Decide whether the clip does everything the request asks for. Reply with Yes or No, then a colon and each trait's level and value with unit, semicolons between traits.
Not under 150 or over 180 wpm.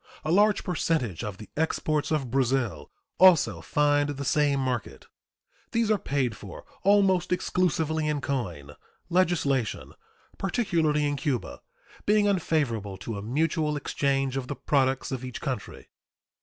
No: slow, 135 wpm